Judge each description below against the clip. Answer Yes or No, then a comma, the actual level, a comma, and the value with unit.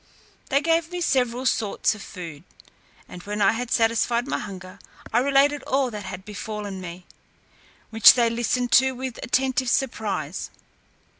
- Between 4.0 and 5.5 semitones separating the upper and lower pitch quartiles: Yes, average, 4.6 semitones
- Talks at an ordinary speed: Yes, average, 150 wpm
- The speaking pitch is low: No, high, 230 Hz